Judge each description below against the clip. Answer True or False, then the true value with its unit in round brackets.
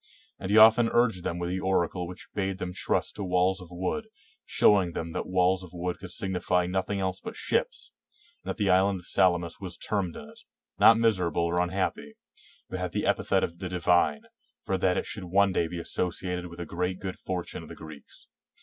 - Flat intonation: True (1.5 semitones)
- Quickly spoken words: True (210 wpm)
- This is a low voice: True (90 Hz)